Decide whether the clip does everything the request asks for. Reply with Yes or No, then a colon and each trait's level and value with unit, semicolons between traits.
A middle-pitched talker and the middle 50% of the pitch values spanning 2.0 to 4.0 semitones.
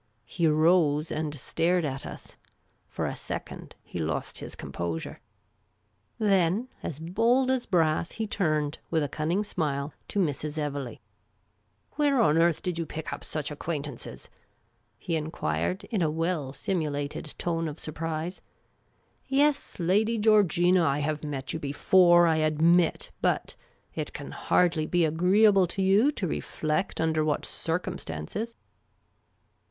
Yes: medium, 165 Hz; average, 3.7 semitones